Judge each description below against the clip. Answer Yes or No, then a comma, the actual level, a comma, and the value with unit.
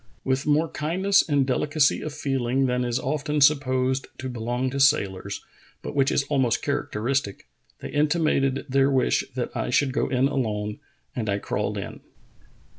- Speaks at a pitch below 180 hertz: Yes, low, 135 Hz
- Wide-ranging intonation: No, average, 2.7 semitones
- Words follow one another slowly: No, average, 165 wpm